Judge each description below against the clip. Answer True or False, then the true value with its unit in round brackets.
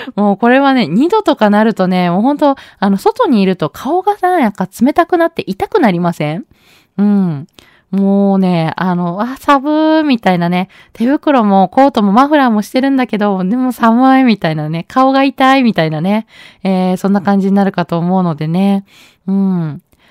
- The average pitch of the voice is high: True (205 Hz)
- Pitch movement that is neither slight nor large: False (6.2 semitones)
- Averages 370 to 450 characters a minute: False (345 characters per minute)